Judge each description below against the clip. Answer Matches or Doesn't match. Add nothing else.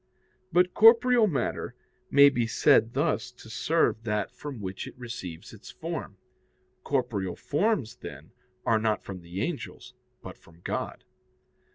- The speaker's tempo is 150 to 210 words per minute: Doesn't match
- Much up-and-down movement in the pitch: Matches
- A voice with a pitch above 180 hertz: Doesn't match